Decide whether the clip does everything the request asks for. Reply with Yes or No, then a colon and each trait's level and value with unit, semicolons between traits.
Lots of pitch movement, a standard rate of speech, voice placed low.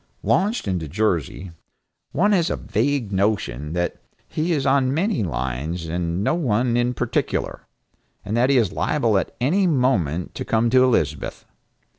Yes: wide, 7.8 semitones; average, 155 wpm; low, 115 Hz